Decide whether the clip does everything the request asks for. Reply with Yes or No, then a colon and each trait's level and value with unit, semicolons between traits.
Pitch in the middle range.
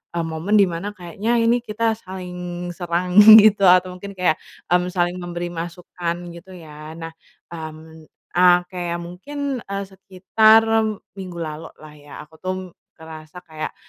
Yes: medium, 180 Hz